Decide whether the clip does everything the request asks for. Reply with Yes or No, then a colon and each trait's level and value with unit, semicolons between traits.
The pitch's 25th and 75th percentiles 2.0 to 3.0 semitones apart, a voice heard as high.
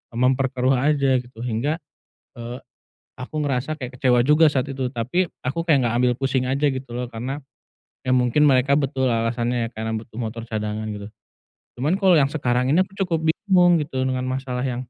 No: average, 2.7 semitones; low, 130 Hz